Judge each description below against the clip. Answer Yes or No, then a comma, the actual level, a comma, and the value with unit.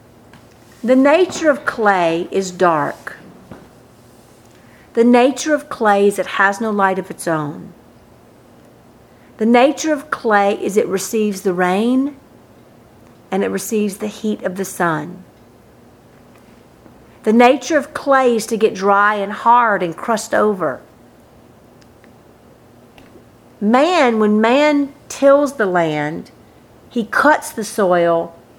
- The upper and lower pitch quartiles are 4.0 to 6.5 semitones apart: Yes, average, 5.1 semitones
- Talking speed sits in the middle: No, slow, 120 wpm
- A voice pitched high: Yes, high, 215 Hz